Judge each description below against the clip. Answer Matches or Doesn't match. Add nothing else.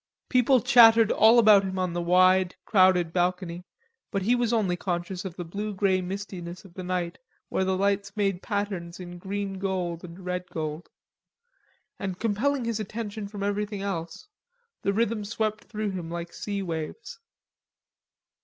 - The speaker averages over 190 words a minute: Doesn't match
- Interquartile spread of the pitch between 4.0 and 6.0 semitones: Doesn't match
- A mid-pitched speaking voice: Doesn't match